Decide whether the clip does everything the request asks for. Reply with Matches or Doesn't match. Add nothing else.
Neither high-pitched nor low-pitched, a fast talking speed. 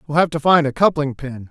Matches